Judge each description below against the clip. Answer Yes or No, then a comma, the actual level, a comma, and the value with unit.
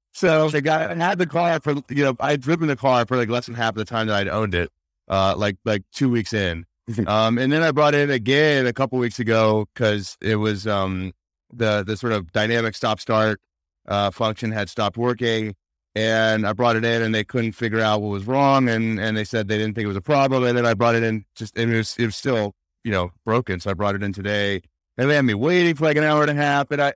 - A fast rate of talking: Yes, fast, 270 wpm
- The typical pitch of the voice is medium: No, low, 115 Hz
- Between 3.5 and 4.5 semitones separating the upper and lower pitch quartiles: Yes, average, 4.0 semitones